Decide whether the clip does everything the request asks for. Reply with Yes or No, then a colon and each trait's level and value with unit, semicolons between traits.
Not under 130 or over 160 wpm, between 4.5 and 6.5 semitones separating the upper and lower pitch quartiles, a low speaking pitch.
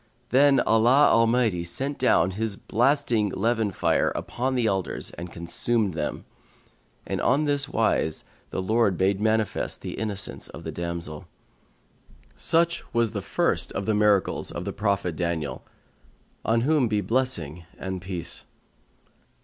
Yes: average, 140 wpm; average, 4.9 semitones; low, 110 Hz